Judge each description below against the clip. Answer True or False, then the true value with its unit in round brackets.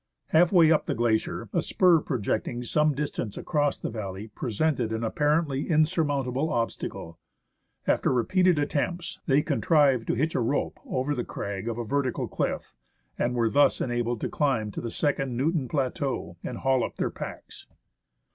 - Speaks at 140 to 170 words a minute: True (165 wpm)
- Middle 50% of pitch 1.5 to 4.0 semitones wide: False (4.4 semitones)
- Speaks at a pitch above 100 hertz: True (135 Hz)